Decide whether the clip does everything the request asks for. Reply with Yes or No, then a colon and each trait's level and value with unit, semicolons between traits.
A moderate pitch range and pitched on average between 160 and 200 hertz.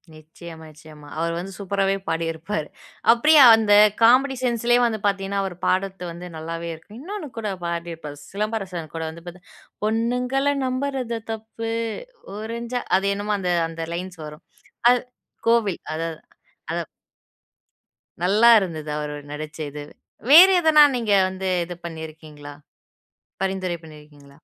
No: wide, 5.9 semitones; high, 190 Hz